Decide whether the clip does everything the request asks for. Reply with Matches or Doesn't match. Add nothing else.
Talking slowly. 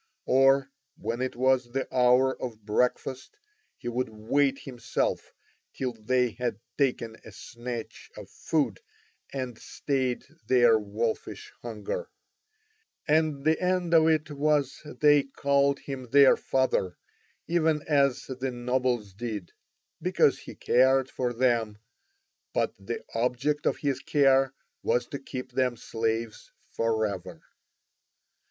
Matches